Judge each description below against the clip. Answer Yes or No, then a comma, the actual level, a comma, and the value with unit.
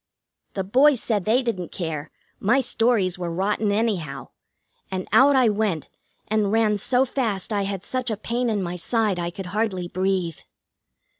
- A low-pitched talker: No, high, 205 Hz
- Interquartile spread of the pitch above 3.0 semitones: Yes, average, 3.8 semitones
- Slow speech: No, average, 165 wpm